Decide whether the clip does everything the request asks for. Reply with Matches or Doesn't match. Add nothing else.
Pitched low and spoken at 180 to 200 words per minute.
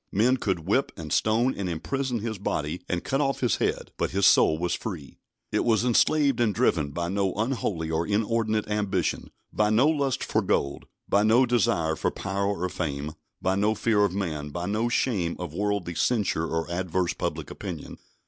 Matches